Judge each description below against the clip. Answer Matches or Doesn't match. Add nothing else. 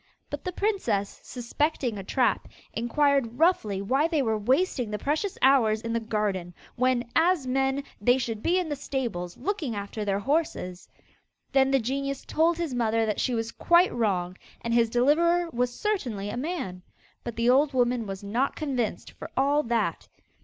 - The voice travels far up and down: Doesn't match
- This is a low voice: Doesn't match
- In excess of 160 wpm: Matches